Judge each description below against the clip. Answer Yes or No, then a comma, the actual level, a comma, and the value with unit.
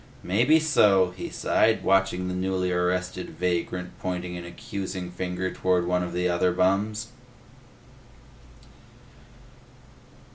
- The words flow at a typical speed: No, slow, 110 wpm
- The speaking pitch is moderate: No, very low, 90 Hz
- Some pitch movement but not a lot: No, narrow, 1.3 semitones